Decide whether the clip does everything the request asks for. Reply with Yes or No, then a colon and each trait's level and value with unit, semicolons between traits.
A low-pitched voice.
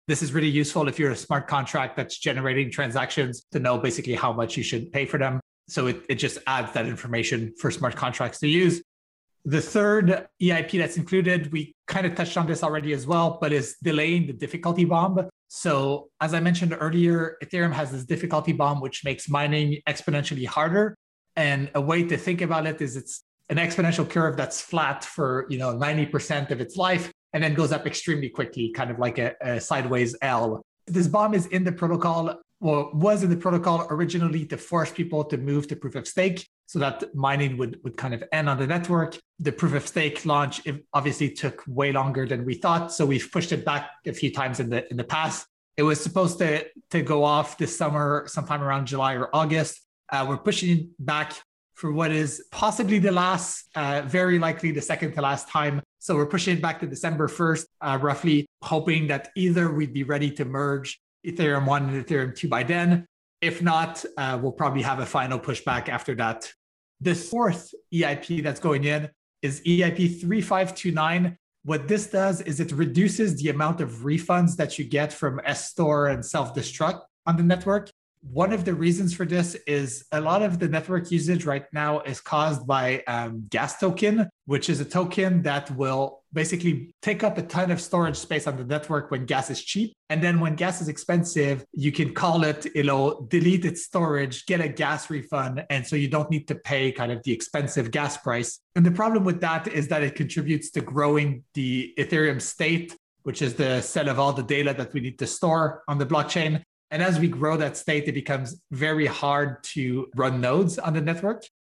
No: medium, 155 Hz